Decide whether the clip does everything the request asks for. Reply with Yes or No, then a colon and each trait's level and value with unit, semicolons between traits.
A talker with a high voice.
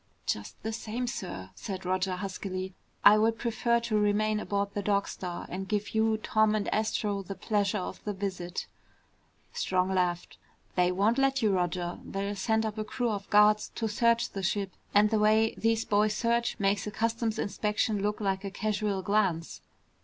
Yes: high, 210 Hz